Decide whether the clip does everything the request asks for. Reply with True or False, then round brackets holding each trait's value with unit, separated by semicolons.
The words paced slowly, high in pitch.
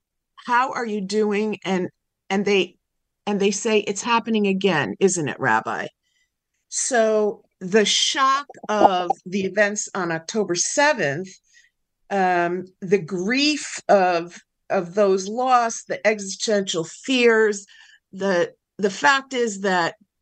True (120 wpm; 205 Hz)